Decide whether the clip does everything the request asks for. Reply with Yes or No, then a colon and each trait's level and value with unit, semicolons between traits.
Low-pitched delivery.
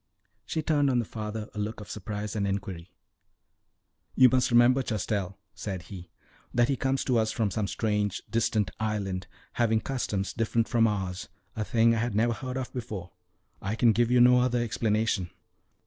Yes: low, 110 Hz